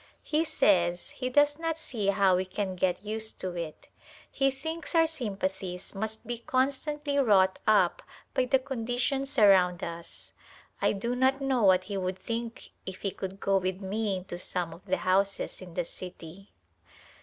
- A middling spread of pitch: No, wide, 5.8 semitones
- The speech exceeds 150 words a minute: Yes, average, 175 wpm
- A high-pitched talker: Yes, high, 200 Hz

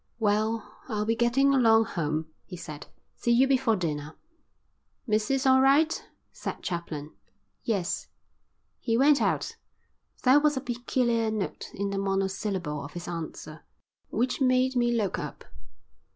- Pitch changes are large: Yes, wide, 5.9 semitones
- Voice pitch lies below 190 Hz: No, high, 220 Hz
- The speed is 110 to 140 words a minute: Yes, slow, 135 wpm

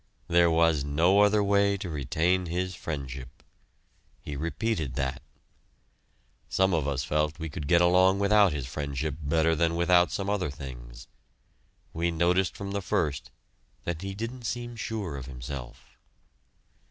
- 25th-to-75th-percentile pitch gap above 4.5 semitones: Yes, average, 5.0 semitones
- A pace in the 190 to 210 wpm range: No, average, 145 wpm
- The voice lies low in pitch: Yes, very low, 85 Hz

